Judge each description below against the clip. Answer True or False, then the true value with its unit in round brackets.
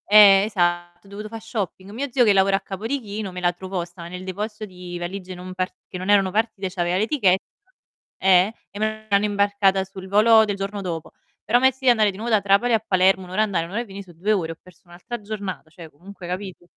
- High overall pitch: True (195 Hz)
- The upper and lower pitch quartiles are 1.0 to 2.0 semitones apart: False (2.7 semitones)